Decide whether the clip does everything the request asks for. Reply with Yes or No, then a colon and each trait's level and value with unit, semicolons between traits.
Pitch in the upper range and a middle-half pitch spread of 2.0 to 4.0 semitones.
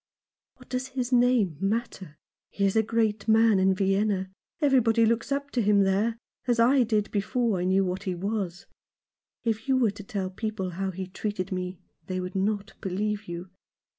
Yes: high, 205 Hz; average, 3.3 semitones